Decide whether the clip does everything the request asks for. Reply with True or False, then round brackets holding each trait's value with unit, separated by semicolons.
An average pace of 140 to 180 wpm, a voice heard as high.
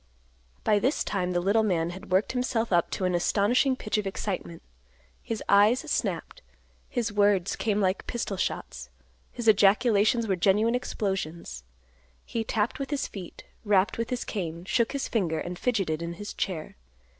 True (165 wpm; 205 Hz)